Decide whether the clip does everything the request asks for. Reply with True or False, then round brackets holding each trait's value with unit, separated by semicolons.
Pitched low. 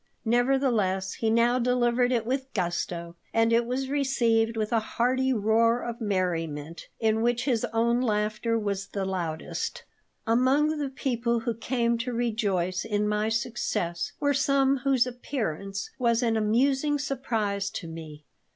False (230 Hz)